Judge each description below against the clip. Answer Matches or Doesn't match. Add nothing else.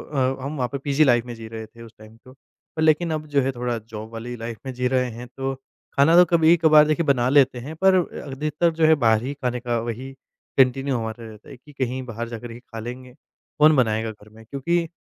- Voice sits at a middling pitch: Doesn't match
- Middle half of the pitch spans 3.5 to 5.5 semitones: Matches